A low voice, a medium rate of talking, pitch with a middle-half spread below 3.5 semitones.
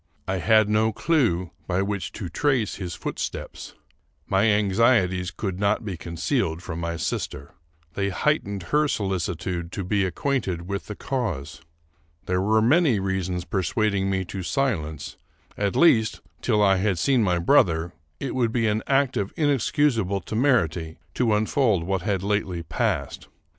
No: low, 100 Hz; average, 150 wpm; average, 4.0 semitones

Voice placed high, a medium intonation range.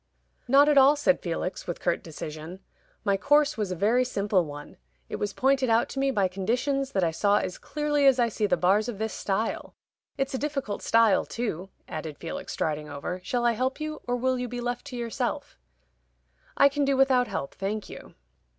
No: high, 230 Hz; wide, 6.1 semitones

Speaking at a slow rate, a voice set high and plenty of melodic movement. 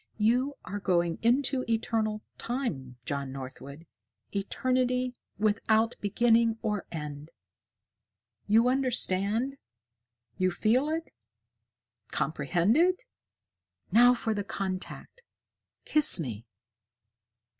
Yes: slow, 90 wpm; high, 220 Hz; wide, 6.1 semitones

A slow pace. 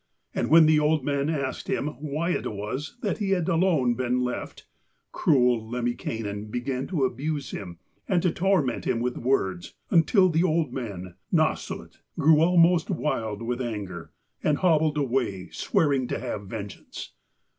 No: average, 155 wpm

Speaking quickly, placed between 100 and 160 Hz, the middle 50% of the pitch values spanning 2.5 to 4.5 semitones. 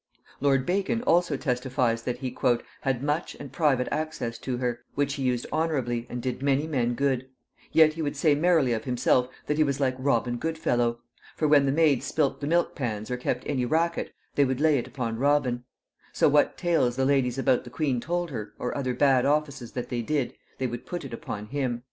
Yes: fast, 210 wpm; low, 135 Hz; average, 3.3 semitones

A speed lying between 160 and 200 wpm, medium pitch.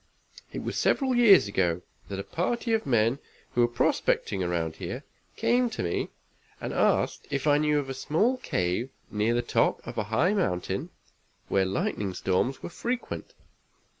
No: average, 165 wpm; low, 120 Hz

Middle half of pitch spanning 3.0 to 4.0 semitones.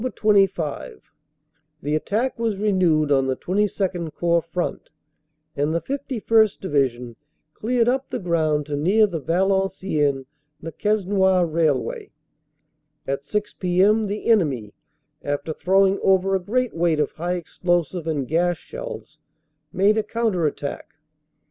No: average, 5.2 semitones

